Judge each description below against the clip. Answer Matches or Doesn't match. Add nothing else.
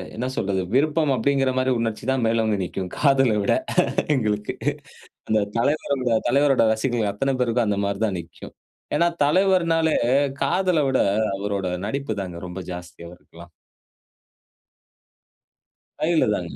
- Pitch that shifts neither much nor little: Doesn't match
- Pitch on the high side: Doesn't match